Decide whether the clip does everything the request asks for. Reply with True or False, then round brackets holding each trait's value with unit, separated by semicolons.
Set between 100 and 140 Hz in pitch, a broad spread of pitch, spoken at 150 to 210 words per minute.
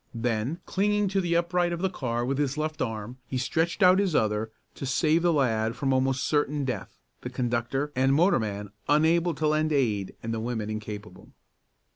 True (135 Hz; 6.3 semitones; 185 wpm)